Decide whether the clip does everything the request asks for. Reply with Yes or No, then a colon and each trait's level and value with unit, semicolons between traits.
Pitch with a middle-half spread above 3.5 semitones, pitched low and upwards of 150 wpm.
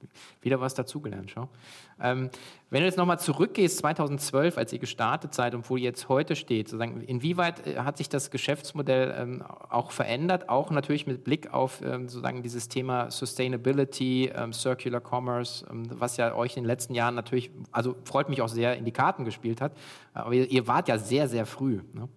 No: average, 2.7 semitones; low, 130 Hz; fast, 190 wpm